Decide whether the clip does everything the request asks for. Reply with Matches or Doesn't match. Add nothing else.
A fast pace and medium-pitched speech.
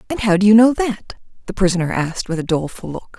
Doesn't match